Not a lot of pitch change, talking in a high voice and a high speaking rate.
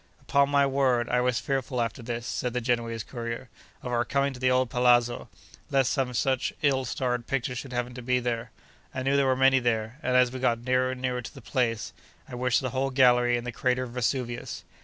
No: narrow, 1.5 semitones; low, 125 Hz; fast, 225 wpm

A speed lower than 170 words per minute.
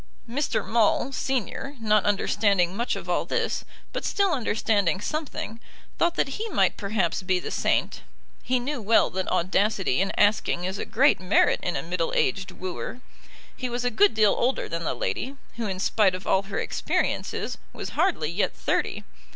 No: average, 175 wpm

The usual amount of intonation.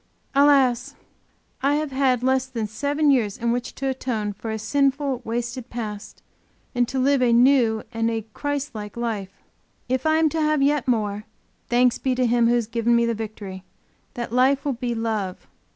Yes: average, 3.2 semitones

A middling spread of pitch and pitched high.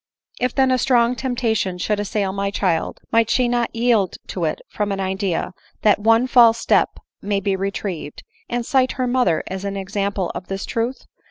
Yes: average, 3.9 semitones; high, 210 Hz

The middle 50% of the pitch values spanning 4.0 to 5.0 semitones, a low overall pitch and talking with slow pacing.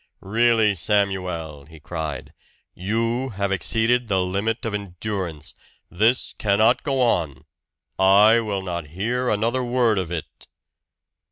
Yes: average, 4.3 semitones; low, 100 Hz; slow, 120 wpm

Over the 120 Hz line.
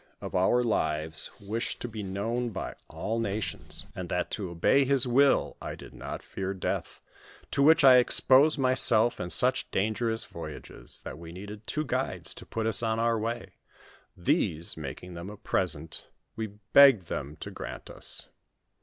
No: low, 110 Hz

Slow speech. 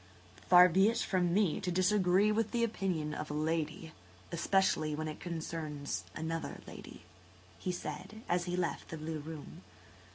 No: average, 155 wpm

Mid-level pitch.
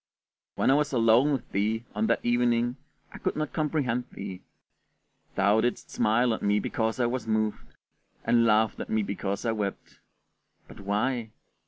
No: low, 115 Hz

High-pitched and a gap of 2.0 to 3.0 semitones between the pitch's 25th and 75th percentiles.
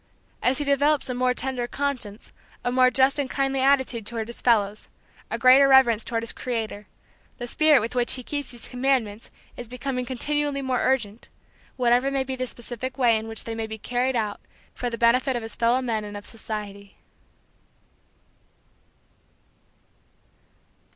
Yes: high, 245 Hz; average, 2.7 semitones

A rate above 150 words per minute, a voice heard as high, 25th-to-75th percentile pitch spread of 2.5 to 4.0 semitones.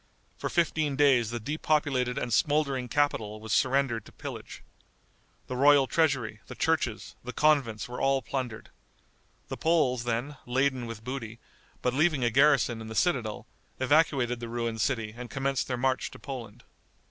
No: average, 160 wpm; low, 130 Hz; average, 3.3 semitones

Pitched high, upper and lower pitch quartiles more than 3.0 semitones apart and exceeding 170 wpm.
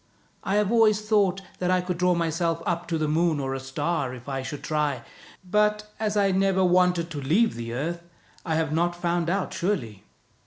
No: medium, 170 Hz; average, 4.1 semitones; average, 200 wpm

